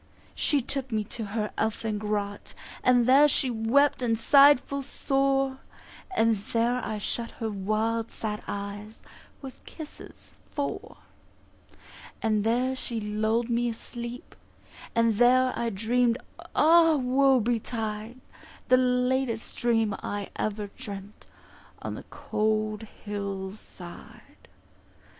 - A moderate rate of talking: No, slow, 120 wpm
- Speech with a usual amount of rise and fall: Yes, average, 3.1 semitones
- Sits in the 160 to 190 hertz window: No, high, 230 Hz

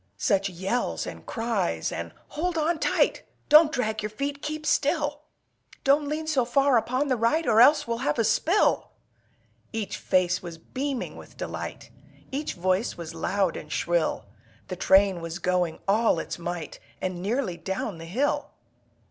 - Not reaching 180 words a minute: Yes, average, 160 wpm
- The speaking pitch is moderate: No, high, 225 Hz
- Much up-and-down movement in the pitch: Yes, wide, 7.9 semitones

